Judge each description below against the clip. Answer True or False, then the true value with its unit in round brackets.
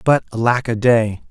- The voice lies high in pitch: False (115 Hz)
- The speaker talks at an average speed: True (185 wpm)